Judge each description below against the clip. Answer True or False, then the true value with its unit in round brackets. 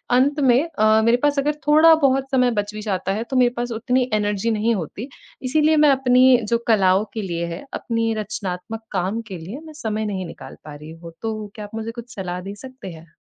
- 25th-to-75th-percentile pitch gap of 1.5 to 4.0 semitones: False (4.5 semitones)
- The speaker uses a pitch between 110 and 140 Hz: False (225 Hz)